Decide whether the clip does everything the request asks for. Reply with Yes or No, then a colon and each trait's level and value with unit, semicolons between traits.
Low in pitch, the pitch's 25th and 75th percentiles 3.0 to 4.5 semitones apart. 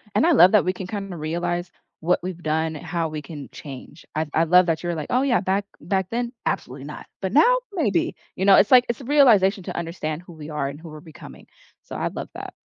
No: medium, 175 Hz; average, 4.2 semitones